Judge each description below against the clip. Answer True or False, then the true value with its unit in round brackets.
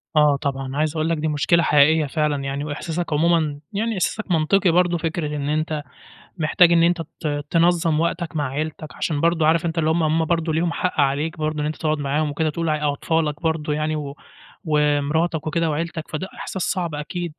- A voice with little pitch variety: True (2.1 semitones)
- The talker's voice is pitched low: False (155 Hz)